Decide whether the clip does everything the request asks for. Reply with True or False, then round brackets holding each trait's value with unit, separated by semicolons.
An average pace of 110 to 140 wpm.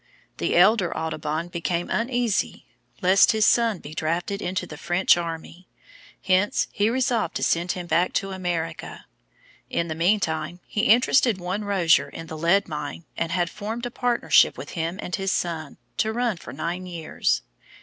False (165 wpm)